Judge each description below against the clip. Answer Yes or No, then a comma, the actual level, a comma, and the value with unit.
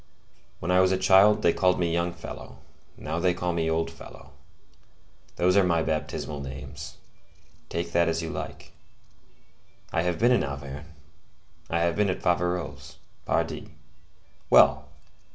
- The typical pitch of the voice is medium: No, very low, 85 Hz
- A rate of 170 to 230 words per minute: No, average, 150 wpm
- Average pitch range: No, narrow, 2.0 semitones